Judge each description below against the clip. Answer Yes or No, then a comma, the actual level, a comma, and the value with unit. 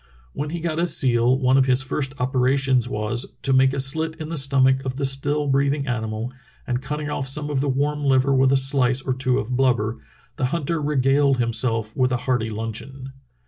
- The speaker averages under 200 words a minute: No, fast, 205 wpm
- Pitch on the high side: No, low, 135 Hz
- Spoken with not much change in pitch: Yes, narrow, 1.9 semitones